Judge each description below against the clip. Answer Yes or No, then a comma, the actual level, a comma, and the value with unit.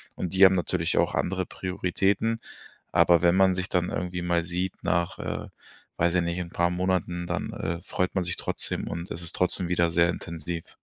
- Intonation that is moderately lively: No, narrow, 1.2 semitones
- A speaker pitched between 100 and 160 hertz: No, very low, 90 Hz